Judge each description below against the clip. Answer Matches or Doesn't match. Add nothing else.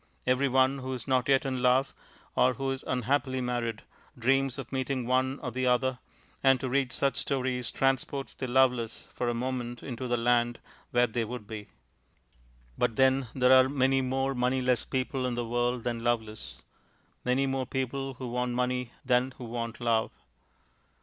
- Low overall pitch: Matches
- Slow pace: Doesn't match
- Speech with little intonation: Matches